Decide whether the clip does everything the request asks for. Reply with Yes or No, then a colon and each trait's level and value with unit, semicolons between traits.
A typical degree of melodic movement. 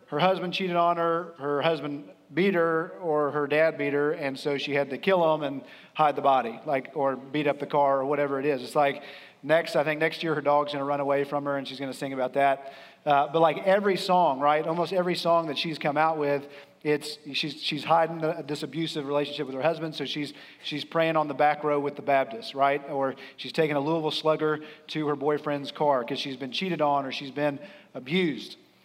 No: narrow, 2.3 semitones